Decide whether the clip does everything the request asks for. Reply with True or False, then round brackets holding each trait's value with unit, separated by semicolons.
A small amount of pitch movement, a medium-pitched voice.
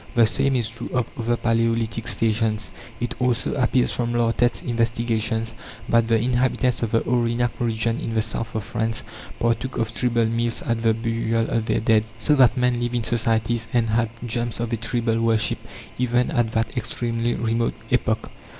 False (1.1 semitones; 115 Hz)